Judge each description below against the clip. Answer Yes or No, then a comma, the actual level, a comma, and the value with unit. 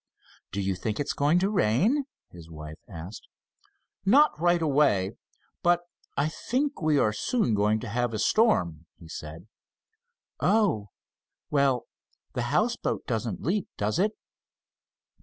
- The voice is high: No, low, 125 Hz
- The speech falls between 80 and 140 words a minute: Yes, slow, 135 wpm